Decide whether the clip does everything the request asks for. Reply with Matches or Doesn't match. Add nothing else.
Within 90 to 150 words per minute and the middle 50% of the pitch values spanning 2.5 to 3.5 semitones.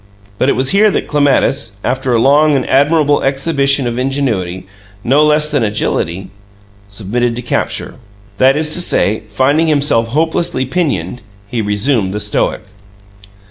Doesn't match